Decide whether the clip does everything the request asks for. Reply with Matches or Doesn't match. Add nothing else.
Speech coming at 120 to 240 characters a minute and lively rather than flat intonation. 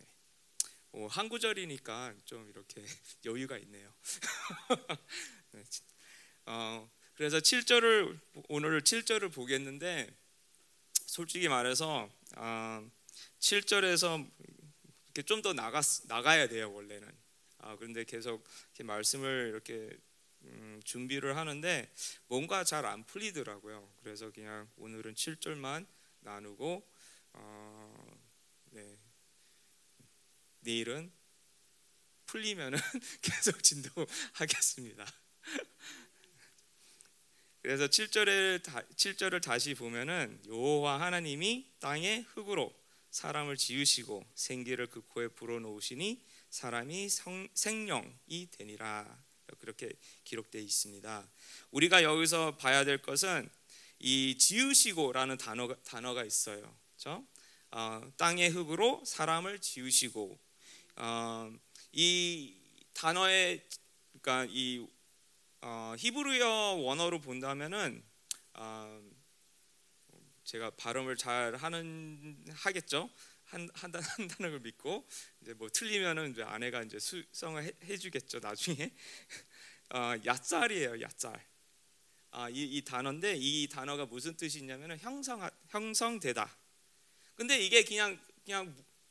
Matches